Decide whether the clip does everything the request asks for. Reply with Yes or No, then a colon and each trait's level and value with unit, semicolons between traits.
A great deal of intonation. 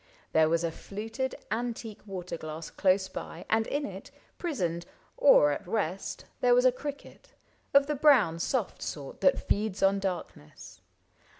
Yes: wide, 6.9 semitones